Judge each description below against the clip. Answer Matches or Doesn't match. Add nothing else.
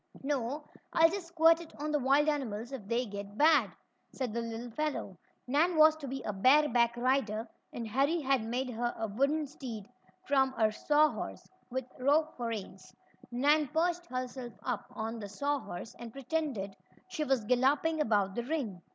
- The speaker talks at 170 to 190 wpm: Matches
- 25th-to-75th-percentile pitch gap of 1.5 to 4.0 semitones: Doesn't match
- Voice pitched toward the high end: Matches